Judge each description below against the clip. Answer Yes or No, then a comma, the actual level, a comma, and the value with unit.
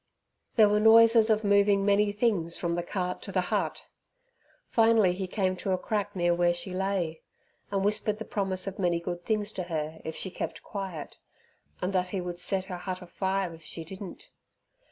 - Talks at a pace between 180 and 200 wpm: Yes, average, 195 wpm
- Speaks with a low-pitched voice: No, high, 190 Hz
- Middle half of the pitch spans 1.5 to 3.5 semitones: Yes, average, 2.7 semitones